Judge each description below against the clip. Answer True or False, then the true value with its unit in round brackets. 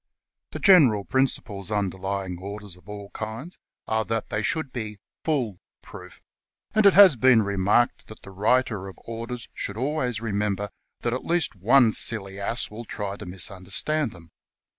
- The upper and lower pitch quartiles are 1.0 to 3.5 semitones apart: False (4.1 semitones)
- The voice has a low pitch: True (110 Hz)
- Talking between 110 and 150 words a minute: False (165 wpm)